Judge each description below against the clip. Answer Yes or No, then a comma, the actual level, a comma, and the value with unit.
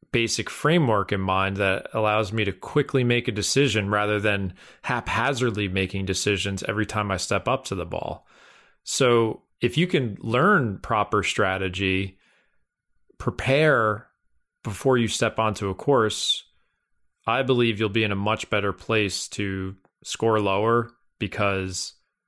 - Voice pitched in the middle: No, low, 105 Hz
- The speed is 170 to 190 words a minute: No, average, 140 wpm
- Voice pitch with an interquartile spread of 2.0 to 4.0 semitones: Yes, average, 3.2 semitones